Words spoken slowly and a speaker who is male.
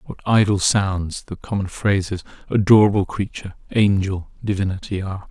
Yes: slow, 125 wpm; male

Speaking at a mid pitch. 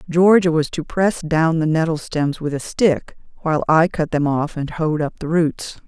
Yes: medium, 160 Hz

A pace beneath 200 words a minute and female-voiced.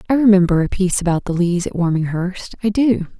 No: fast, 205 wpm; female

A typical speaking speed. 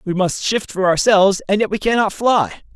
No: fast, 220 wpm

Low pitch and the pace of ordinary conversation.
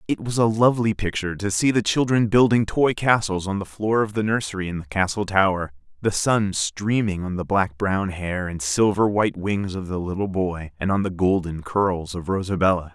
No: low, 100 Hz; fast, 210 wpm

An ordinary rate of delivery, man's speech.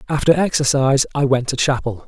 Yes: average, 175 wpm; male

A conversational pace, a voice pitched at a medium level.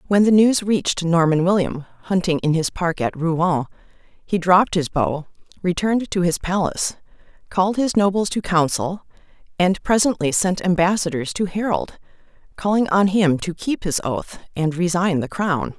Yes: average, 160 wpm; medium, 180 Hz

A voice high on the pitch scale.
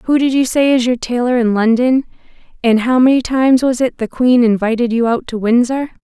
Yes: high, 245 Hz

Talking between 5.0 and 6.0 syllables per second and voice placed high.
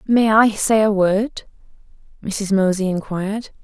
No: 4.1 syllables/s; high, 205 Hz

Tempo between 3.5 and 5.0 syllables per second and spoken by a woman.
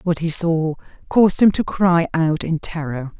Yes: 4.5 syllables/s; female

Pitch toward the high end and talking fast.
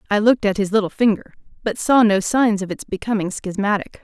Yes: high, 210 Hz; fast, 210 wpm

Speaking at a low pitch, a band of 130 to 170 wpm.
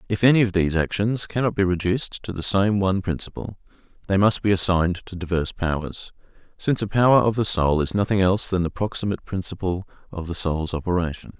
No: very low, 95 Hz; average, 195 wpm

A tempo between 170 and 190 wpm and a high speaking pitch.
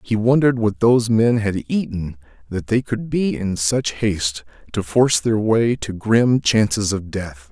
No: average, 185 wpm; low, 105 Hz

